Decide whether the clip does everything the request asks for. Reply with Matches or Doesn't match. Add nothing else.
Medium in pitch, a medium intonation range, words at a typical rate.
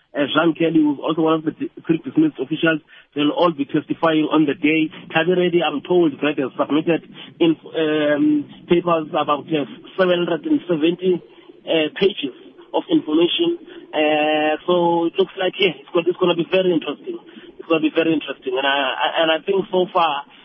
Matches